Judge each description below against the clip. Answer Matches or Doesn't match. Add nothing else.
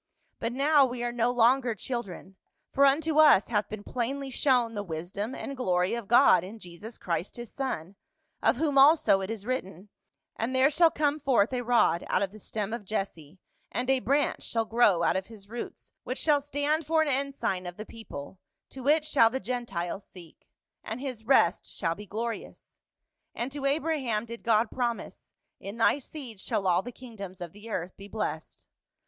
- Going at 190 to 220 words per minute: Matches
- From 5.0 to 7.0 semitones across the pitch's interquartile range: Matches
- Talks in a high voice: Matches